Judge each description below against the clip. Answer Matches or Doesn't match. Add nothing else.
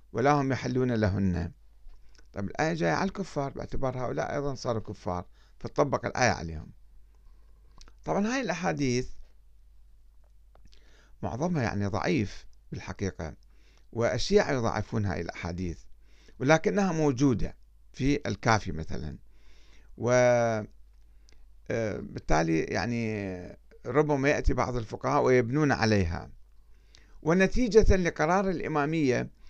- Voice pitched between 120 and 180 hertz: Doesn't match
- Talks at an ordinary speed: Matches